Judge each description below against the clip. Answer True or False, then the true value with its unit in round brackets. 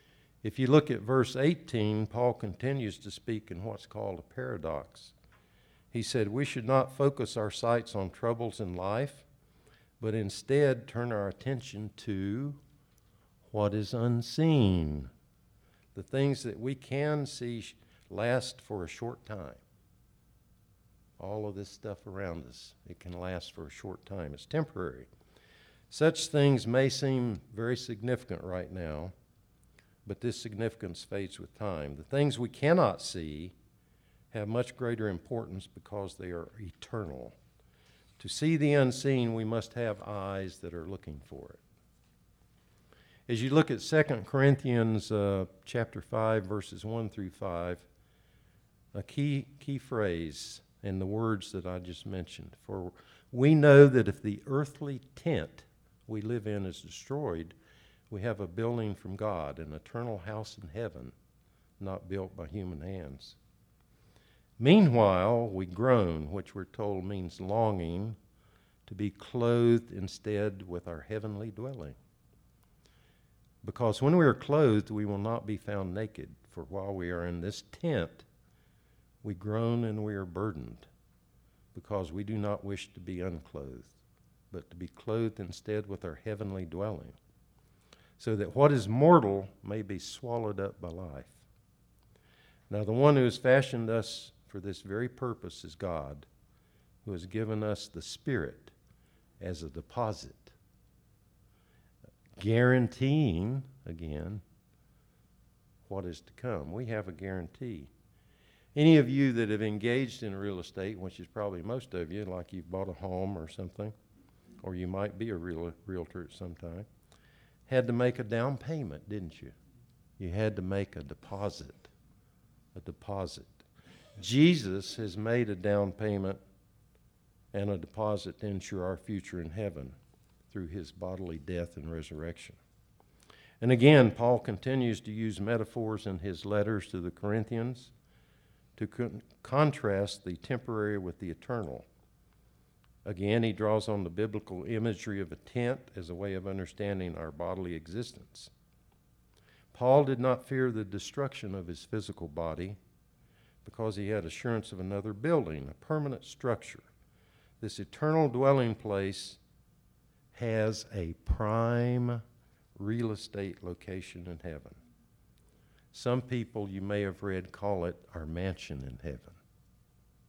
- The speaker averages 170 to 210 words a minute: False (145 wpm)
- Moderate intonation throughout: True (4.4 semitones)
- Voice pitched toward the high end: False (105 Hz)